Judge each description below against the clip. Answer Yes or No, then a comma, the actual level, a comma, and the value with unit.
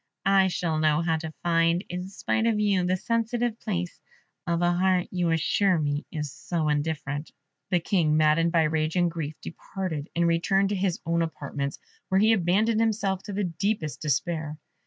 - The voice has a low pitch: No, medium, 175 Hz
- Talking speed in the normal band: Yes, average, 180 wpm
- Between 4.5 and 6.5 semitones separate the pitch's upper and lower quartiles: No, average, 3.5 semitones